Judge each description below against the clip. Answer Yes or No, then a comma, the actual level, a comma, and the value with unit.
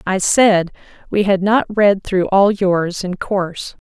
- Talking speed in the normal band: Yes, average, 170 wpm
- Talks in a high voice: Yes, high, 195 Hz